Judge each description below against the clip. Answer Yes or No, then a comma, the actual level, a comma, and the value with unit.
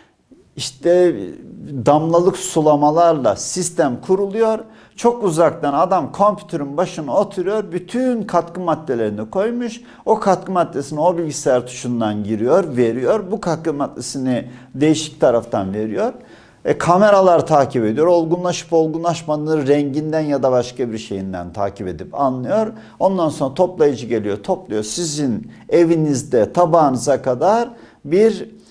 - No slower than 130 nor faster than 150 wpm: No, average, 115 wpm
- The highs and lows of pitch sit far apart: Yes, wide, 5.8 semitones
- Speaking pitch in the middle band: Yes, medium, 160 Hz